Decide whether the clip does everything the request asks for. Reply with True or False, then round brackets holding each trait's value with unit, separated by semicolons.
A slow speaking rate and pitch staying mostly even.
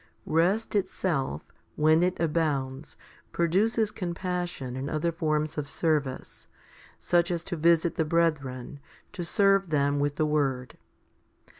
False (130 wpm; 3.4 semitones)